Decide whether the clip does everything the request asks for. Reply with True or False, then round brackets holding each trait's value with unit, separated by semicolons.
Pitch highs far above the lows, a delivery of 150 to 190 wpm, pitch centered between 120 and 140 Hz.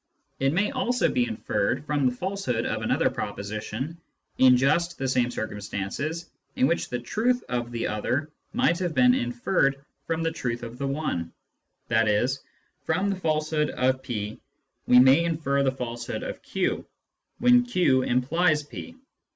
True (5.7 semitones; 155 wpm; 135 Hz)